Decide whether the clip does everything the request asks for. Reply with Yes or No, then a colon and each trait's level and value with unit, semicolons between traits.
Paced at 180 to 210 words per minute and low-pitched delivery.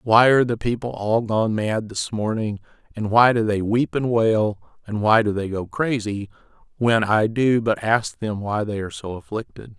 Yes: average, 200 wpm; low, 110 Hz